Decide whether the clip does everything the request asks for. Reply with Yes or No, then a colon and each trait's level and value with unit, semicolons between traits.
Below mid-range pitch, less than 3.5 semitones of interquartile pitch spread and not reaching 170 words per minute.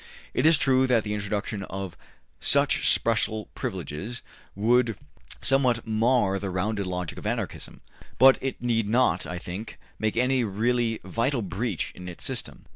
No: low, 110 Hz; average, 4.0 semitones; average, 150 wpm